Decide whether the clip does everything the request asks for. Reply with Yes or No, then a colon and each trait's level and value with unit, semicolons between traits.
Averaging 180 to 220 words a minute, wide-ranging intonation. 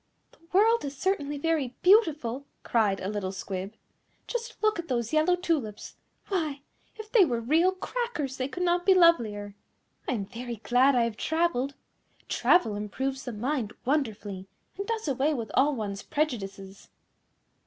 No: average, 155 wpm; wide, 7.5 semitones